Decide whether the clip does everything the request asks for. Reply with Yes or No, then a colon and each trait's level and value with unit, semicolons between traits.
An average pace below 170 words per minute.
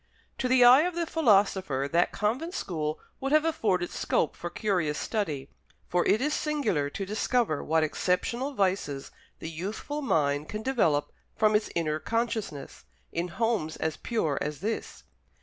Yes: average, 155 wpm